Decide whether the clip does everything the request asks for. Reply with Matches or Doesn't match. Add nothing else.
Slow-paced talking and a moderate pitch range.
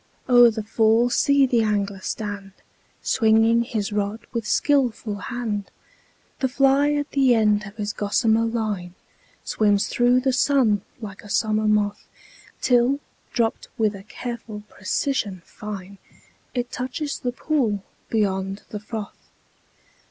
Matches